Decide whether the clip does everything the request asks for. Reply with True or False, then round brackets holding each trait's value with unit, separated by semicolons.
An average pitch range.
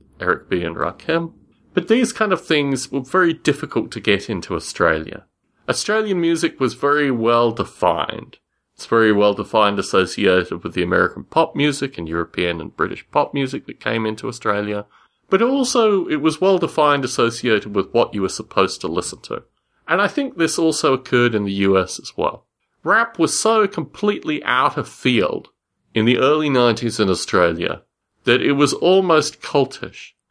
False (6.8 semitones)